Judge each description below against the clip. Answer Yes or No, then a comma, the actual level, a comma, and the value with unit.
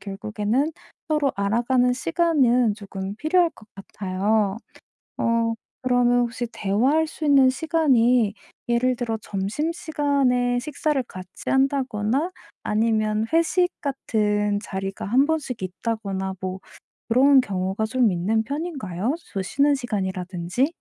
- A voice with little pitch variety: No, average, 5.2 semitones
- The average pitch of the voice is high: Yes, high, 235 Hz